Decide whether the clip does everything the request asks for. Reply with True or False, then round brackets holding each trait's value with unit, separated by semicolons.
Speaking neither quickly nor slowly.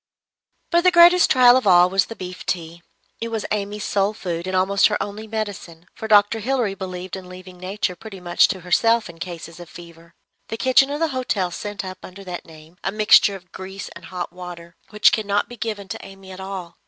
False (215 wpm)